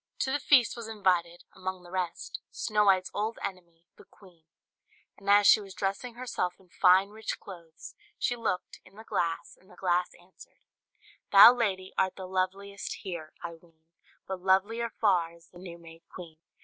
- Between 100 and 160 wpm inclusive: No, average, 175 wpm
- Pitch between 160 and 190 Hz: Yes, medium, 185 Hz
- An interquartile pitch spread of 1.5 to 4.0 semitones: Yes, average, 2.7 semitones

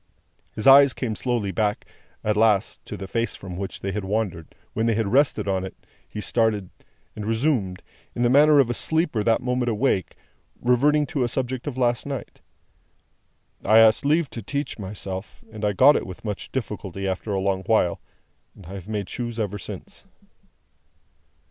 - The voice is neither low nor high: No, low, 110 Hz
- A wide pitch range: No, average, 4.2 semitones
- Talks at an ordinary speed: Yes, average, 180 wpm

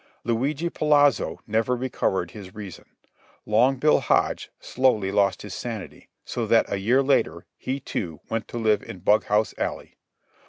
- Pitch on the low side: Yes, low, 115 Hz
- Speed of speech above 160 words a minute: No, average, 150 wpm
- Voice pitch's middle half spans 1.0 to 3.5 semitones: No, average, 4.4 semitones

